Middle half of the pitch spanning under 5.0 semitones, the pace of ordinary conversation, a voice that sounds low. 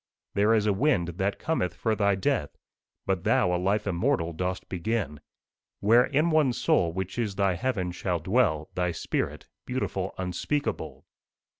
Yes: average, 4.6 semitones; average, 155 wpm; very low, 95 Hz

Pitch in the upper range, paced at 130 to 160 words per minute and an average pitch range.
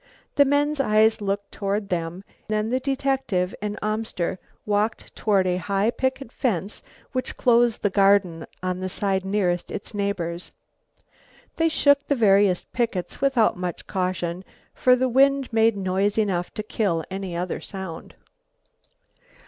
Yes: high, 205 Hz; average, 140 wpm; average, 4.2 semitones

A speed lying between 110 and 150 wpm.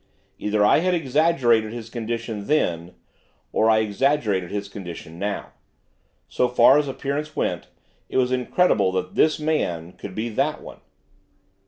Yes: average, 145 wpm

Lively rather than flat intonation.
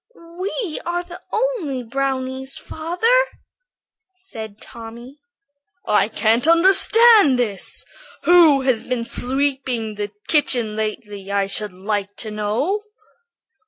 Yes: wide, 7.7 semitones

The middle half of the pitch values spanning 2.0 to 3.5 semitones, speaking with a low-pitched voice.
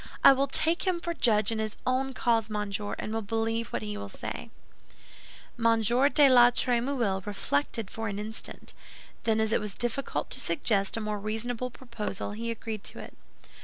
No: average, 2.7 semitones; high, 225 Hz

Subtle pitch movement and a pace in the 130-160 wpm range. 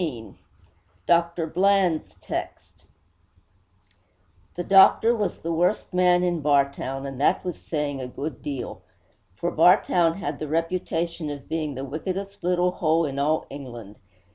No: average, 4.1 semitones; average, 140 wpm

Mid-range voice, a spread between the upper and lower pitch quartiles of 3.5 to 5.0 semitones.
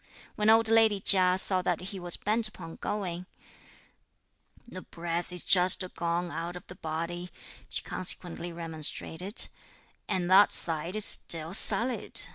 No: medium, 180 Hz; average, 2.7 semitones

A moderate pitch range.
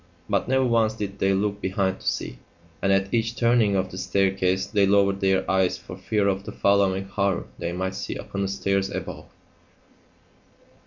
No: narrow, 1.2 semitones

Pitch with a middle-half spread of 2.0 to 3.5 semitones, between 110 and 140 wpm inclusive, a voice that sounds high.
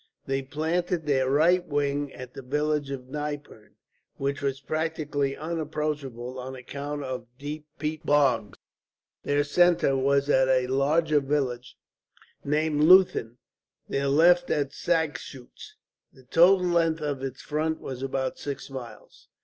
No: average, 2.7 semitones; slow, 135 wpm; medium, 145 Hz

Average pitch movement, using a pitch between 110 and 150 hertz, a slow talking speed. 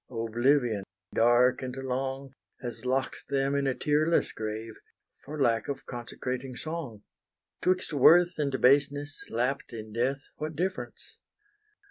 Yes: average, 3.1 semitones; low, 135 Hz; slow, 125 wpm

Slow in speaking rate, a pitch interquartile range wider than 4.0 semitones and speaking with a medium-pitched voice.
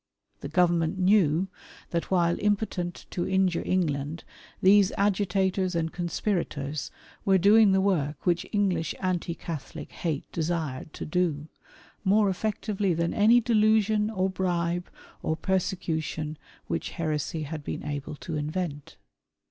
No: slow, 125 wpm; average, 3.5 semitones; medium, 175 Hz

